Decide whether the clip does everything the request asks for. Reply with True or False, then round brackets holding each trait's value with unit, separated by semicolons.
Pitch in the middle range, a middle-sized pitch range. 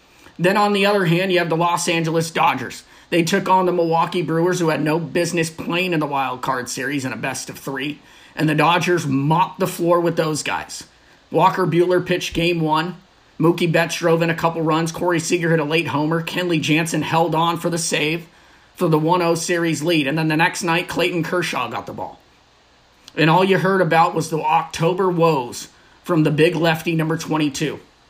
False (165 Hz; 1.8 semitones)